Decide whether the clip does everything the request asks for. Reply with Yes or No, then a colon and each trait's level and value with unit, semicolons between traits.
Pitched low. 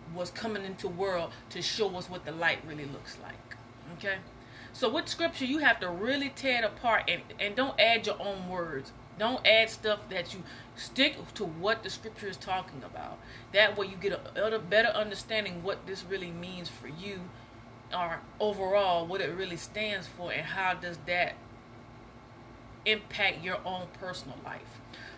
No: medium, 180 Hz